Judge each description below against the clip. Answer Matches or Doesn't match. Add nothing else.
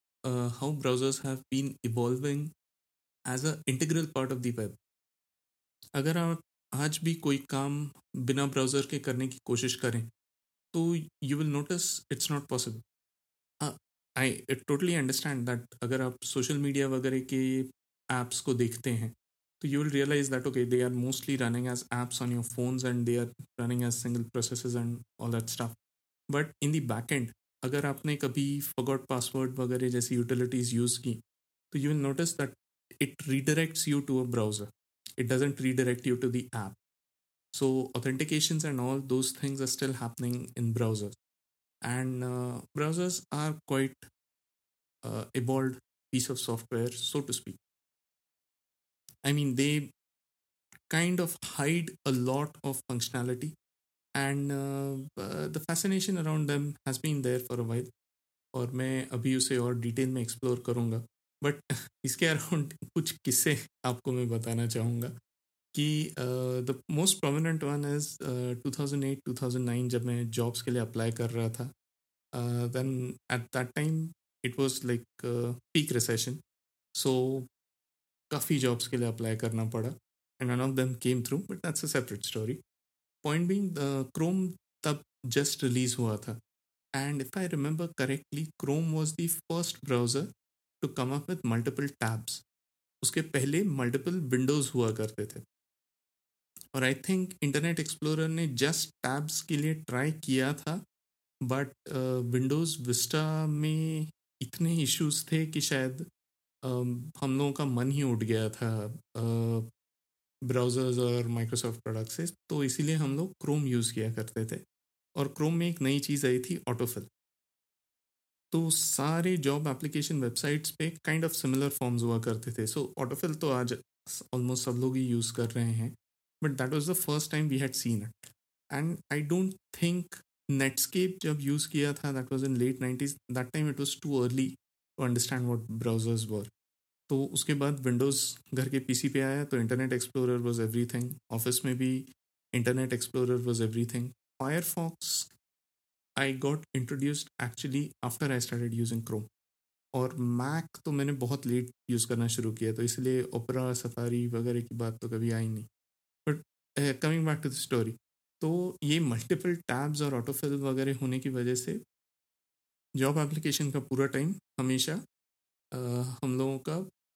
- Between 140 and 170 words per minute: Matches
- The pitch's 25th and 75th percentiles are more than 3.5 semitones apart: Doesn't match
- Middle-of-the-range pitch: Doesn't match